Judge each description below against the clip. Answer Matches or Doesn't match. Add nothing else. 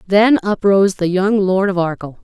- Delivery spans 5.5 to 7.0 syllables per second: Doesn't match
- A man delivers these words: Doesn't match